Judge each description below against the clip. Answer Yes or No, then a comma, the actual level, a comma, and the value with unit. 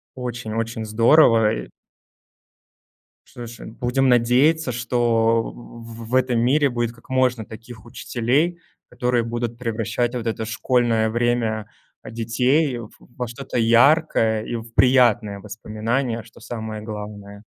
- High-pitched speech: No, low, 115 Hz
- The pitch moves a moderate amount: No, narrow, 1.8 semitones